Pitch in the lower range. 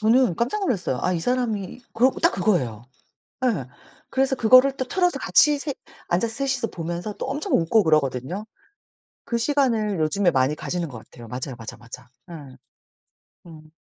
No: high, 200 Hz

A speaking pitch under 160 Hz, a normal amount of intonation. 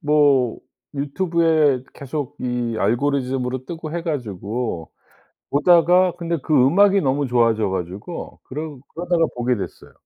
Yes: medium, 140 Hz; average, 5.0 semitones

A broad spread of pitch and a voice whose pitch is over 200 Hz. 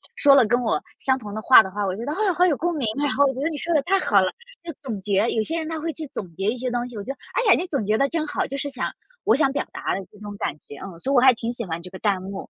Yes: wide, 6.1 semitones; very high, 250 Hz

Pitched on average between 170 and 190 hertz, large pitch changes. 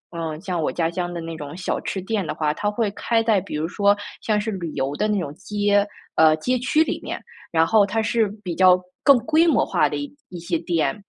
No: medium, 185 Hz; average, 4.5 semitones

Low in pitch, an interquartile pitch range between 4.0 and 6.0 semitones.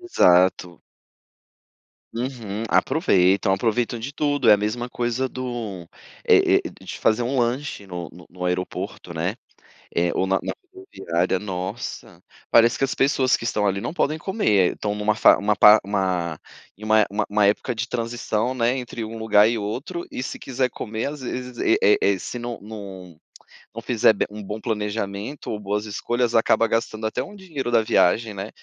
No: low, 110 Hz; average, 3.5 semitones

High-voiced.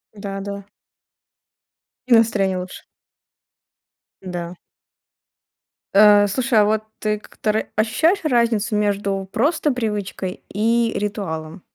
Yes: high, 210 Hz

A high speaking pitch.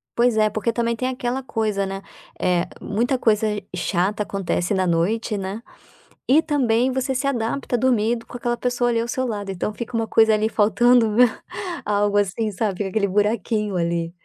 Yes: high, 220 Hz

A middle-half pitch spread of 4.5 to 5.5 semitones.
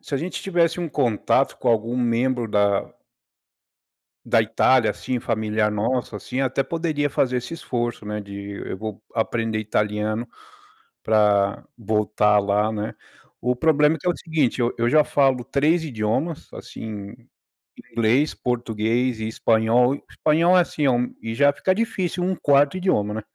Yes: average, 5.0 semitones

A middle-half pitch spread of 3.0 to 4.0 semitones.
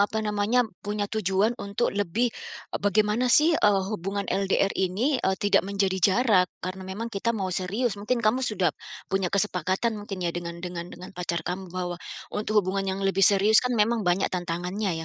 No: narrow, 2.6 semitones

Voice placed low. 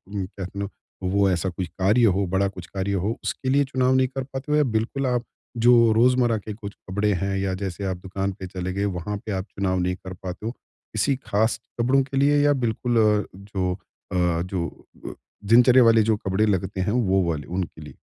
Yes: low, 100 Hz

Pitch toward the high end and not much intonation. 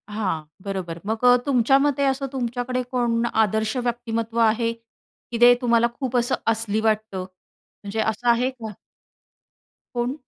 Yes: high, 230 Hz; narrow, 2.1 semitones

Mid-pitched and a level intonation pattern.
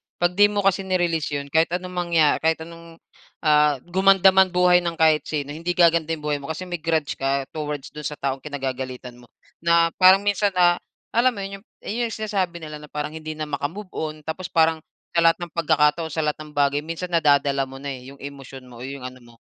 No: medium, 160 Hz; average, 3.6 semitones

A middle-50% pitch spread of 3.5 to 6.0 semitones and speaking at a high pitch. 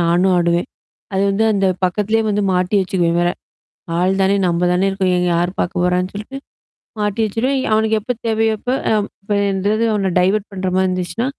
No: average, 2.9 semitones; high, 195 Hz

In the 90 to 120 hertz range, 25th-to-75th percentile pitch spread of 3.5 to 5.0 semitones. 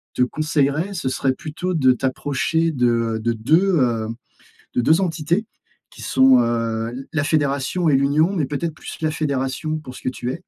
No: medium, 140 Hz; average, 3.8 semitones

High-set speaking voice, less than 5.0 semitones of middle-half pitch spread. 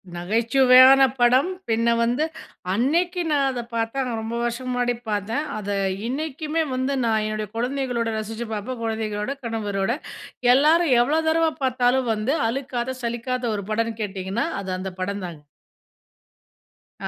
Yes: high, 240 Hz; average, 3.5 semitones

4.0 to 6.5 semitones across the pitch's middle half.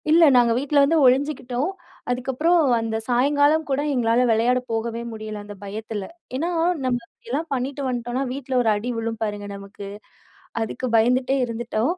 No: average, 3.3 semitones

